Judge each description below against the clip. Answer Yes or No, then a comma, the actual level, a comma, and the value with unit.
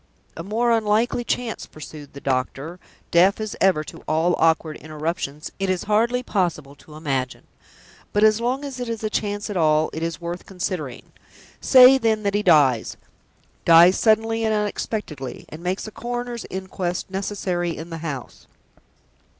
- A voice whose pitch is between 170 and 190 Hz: Yes, medium, 185 Hz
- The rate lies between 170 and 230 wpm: No, average, 160 wpm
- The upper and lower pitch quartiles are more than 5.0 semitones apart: Yes, wide, 5.6 semitones